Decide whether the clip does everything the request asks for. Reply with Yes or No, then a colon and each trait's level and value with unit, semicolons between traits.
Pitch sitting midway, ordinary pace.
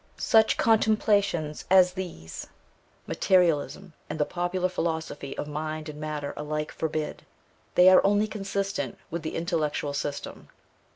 No: medium, 165 Hz; slow, 125 wpm